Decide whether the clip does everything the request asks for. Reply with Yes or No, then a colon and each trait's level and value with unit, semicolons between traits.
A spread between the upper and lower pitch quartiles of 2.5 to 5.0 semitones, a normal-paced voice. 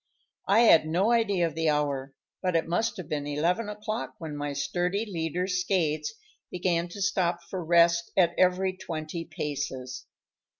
Yes: average, 3.3 semitones; average, 160 wpm